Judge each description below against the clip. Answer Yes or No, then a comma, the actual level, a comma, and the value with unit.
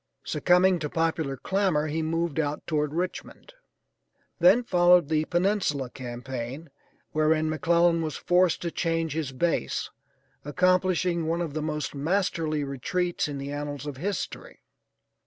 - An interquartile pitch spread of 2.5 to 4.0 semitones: Yes, average, 3.2 semitones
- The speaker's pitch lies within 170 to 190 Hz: No, medium, 160 Hz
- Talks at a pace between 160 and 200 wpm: No, slow, 135 wpm